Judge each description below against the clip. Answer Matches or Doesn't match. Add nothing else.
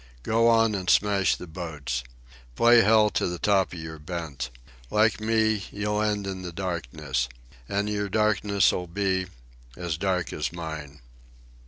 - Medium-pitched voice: Doesn't match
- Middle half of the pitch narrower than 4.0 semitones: Doesn't match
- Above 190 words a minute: Doesn't match